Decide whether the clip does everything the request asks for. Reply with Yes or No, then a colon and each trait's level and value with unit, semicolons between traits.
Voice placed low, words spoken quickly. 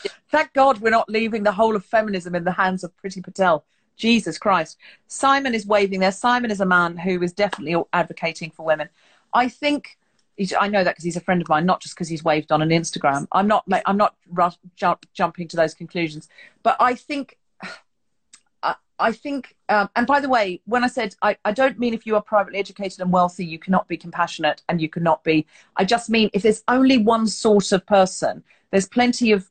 No: high, 195 Hz; fast, 220 wpm